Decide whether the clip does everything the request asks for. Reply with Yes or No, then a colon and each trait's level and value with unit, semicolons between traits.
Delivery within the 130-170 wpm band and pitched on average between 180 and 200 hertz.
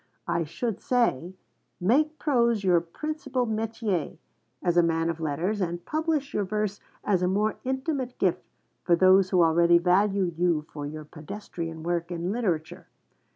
Yes: average, 155 wpm; medium, 185 Hz